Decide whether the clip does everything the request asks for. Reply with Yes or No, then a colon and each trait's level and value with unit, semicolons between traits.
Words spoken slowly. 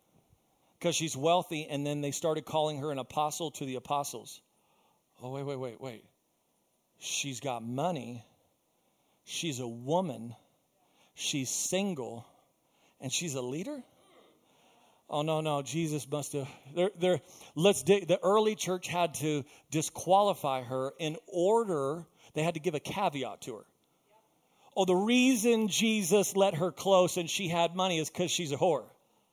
No: average, 145 wpm